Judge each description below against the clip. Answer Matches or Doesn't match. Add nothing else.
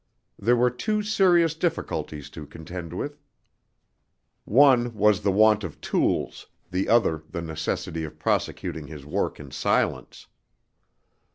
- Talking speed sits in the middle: Doesn't match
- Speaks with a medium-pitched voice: Doesn't match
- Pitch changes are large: Matches